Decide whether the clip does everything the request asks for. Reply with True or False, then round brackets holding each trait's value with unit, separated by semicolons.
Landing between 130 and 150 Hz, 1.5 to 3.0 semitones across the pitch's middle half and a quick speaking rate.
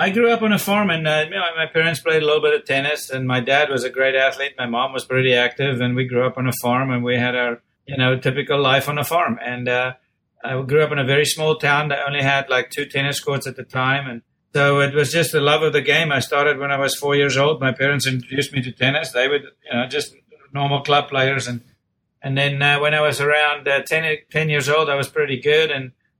True (140 Hz; 2.4 semitones; 270 wpm)